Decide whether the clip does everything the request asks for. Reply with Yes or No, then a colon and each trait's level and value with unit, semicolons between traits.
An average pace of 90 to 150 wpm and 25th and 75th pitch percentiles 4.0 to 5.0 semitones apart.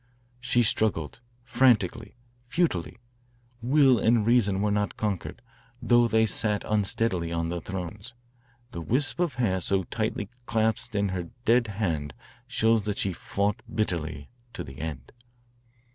Yes: slow, 135 wpm; average, 4.5 semitones